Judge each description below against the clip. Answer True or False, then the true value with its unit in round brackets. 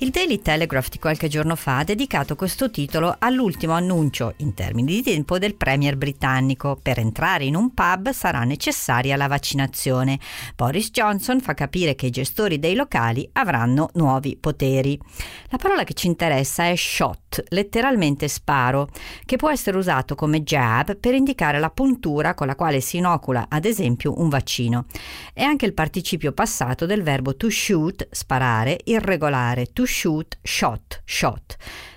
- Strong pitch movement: True (5.9 semitones)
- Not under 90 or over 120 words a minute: False (160 wpm)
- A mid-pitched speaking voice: True (150 Hz)